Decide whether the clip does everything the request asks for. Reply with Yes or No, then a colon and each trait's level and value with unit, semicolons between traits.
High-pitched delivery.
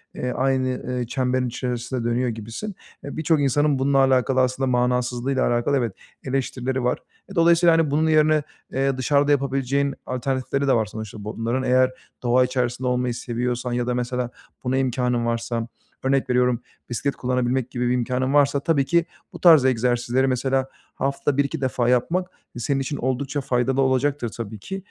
No: low, 130 Hz